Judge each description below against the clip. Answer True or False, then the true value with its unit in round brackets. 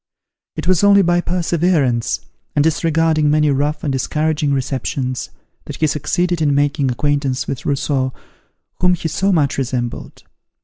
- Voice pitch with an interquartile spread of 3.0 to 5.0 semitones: True (3.4 semitones)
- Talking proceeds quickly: False (140 wpm)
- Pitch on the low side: False (150 Hz)